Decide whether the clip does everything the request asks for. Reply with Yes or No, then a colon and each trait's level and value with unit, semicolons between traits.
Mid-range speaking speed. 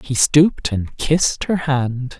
Yes: average, 165 wpm